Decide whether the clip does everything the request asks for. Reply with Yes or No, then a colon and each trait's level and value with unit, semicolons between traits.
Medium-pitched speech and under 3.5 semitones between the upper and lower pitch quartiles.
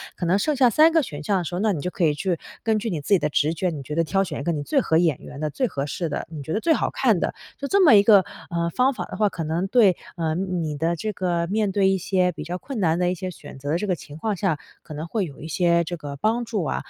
No: medium, 180 Hz; average, 4.6 semitones